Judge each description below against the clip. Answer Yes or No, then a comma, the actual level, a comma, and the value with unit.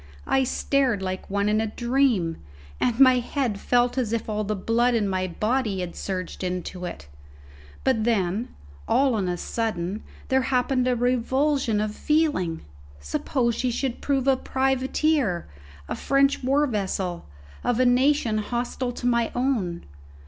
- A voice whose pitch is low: No, high, 235 Hz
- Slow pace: No, average, 155 wpm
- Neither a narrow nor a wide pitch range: Yes, average, 4.7 semitones